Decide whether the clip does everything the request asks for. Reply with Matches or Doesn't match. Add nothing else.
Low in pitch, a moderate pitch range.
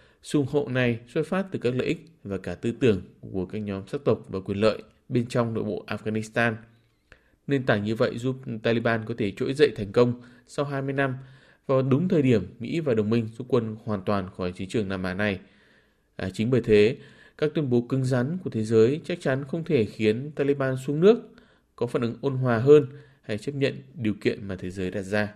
Matches